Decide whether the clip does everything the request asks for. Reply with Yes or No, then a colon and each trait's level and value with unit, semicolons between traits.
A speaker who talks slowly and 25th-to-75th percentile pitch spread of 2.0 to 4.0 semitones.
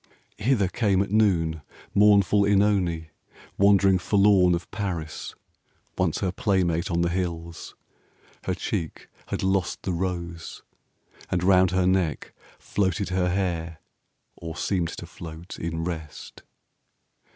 Yes: slow, 125 wpm; average, 2.7 semitones